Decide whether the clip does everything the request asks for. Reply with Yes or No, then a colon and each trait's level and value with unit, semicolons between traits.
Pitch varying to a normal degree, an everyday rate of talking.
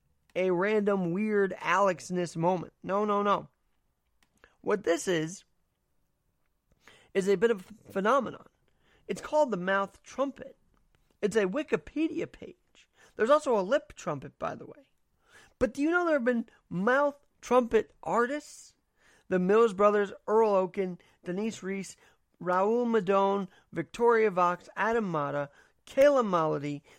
No: average, 4.7 semitones; slow, 130 wpm